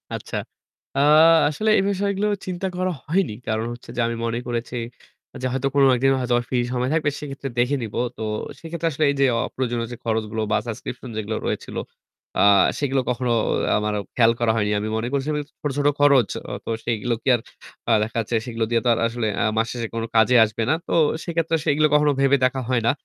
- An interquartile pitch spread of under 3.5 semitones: No, average, 4.3 semitones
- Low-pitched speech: Yes, low, 125 Hz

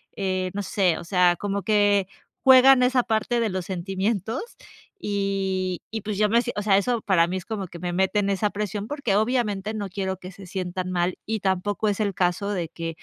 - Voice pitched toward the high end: Yes, high, 195 Hz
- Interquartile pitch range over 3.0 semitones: No, narrow, 2.4 semitones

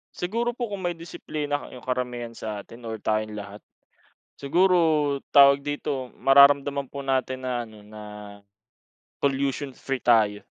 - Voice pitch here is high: No, low, 135 Hz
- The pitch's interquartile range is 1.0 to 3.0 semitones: No, average, 3.6 semitones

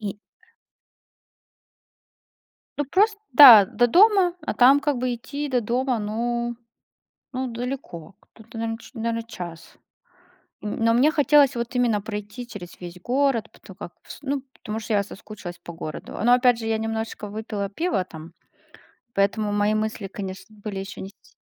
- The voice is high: Yes, high, 225 Hz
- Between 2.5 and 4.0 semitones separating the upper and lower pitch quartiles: Yes, average, 3.5 semitones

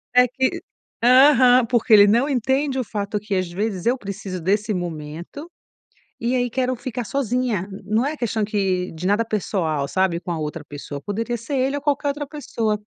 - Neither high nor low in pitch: No, high, 220 Hz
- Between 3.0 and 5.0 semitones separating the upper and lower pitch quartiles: No, wide, 5.4 semitones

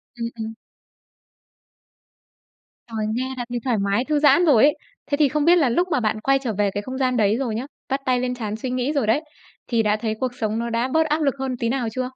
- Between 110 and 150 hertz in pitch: No, very high, 250 Hz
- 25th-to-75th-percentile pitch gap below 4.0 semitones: Yes, average, 3.4 semitones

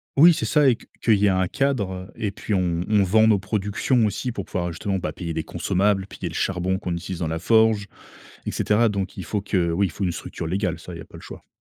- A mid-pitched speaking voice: No, very low, 95 Hz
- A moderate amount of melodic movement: Yes, average, 3.1 semitones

